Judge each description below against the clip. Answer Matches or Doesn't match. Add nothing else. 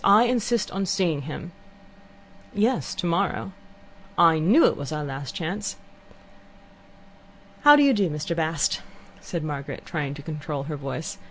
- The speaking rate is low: Doesn't match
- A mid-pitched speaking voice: Matches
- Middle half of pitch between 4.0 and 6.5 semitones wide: Matches